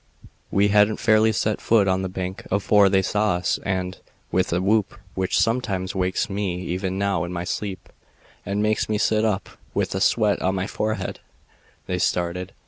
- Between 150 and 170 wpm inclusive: No, average, 180 wpm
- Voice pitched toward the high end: No, very low, 95 Hz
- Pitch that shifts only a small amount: Yes, narrow, 2.3 semitones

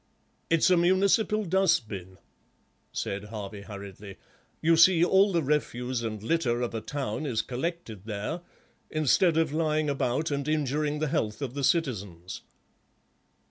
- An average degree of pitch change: No, wide, 7.1 semitones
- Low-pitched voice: No, medium, 145 Hz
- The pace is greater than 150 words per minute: No, average, 140 wpm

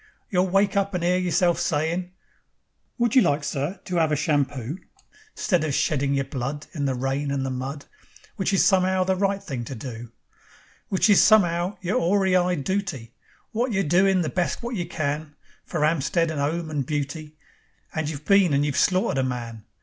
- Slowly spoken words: No, average, 190 wpm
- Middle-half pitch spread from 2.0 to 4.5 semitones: No, average, 4.9 semitones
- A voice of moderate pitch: Yes, medium, 160 Hz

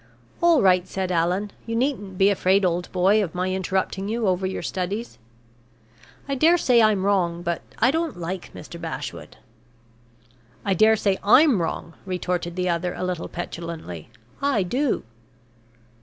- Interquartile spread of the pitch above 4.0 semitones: No, average, 3.5 semitones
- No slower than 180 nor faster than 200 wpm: No, average, 155 wpm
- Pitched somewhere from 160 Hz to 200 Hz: Yes, high, 190 Hz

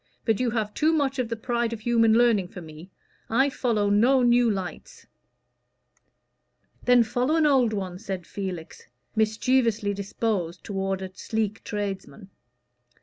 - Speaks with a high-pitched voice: Yes, high, 220 Hz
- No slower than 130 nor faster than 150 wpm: Yes, average, 145 wpm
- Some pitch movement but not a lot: Yes, average, 3.7 semitones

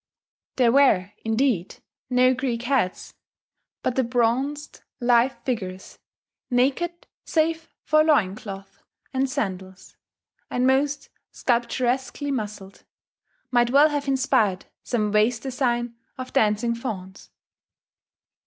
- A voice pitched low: No, high, 245 Hz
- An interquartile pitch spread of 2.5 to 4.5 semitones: Yes, average, 4.0 semitones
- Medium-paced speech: No, slow, 105 wpm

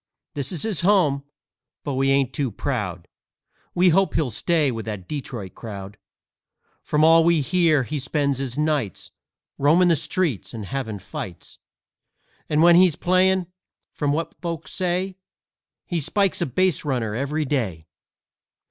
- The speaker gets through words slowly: No, average, 150 wpm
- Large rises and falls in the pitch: Yes, wide, 5.7 semitones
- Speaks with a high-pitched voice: No, medium, 145 Hz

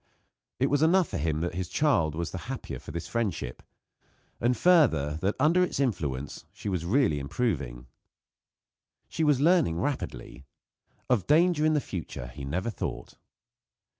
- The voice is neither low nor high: No, low, 100 Hz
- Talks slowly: No, average, 155 wpm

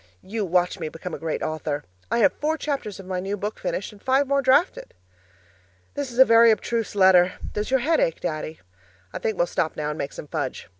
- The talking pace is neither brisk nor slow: No, fast, 220 wpm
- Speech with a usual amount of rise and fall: No, wide, 7.2 semitones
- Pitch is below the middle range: No, high, 200 Hz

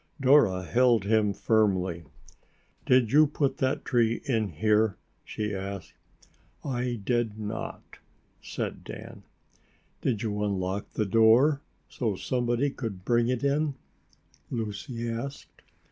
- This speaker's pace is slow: Yes, slow, 115 wpm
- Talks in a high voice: No, low, 115 Hz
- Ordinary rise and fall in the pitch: Yes, average, 3.6 semitones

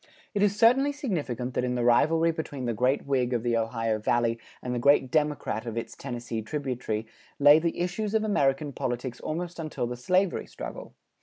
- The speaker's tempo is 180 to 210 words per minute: Yes, average, 185 wpm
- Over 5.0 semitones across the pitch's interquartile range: Yes, wide, 5.5 semitones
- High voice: No, low, 135 Hz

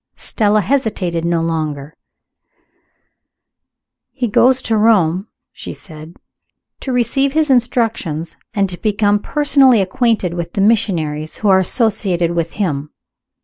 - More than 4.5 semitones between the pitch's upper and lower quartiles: Yes, wide, 5.5 semitones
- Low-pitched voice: No, high, 200 Hz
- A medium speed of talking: No, slow, 120 wpm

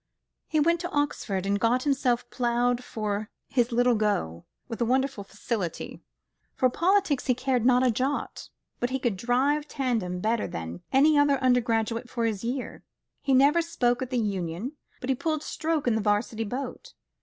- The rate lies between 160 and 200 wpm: Yes, average, 175 wpm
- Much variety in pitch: No, average, 3.8 semitones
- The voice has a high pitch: Yes, high, 245 Hz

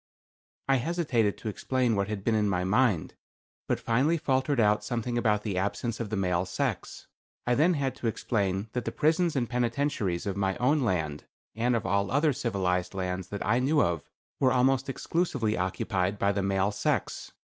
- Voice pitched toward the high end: No, low, 110 Hz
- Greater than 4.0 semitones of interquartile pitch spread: Yes, average, 5.0 semitones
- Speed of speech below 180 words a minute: No, average, 185 wpm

